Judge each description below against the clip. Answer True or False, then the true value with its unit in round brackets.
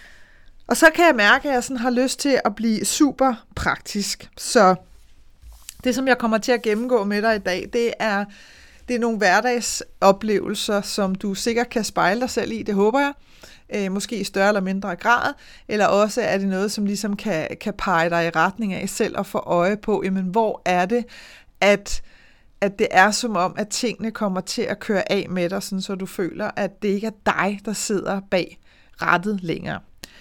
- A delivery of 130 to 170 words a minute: False (205 wpm)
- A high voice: True (205 Hz)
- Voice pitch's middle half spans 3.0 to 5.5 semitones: True (3.3 semitones)